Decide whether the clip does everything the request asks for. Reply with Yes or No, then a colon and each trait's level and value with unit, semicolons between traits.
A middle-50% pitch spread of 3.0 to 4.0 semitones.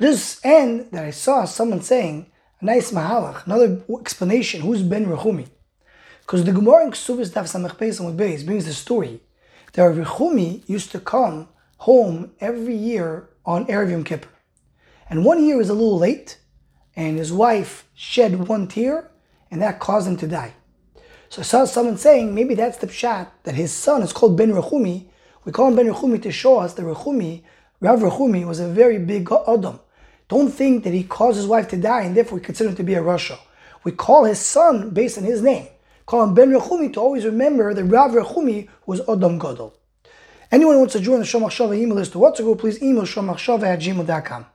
No: average, 5.3 semitones